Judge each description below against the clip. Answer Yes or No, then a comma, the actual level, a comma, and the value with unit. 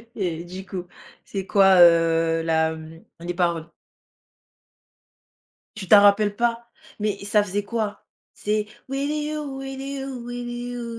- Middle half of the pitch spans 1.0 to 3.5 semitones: No, wide, 5.6 semitones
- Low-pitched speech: No, high, 205 Hz